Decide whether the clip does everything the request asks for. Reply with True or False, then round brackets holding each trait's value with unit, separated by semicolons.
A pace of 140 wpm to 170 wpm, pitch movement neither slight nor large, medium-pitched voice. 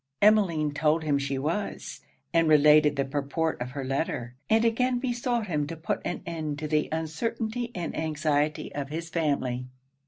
True (165 wpm; 3.4 semitones; 155 Hz)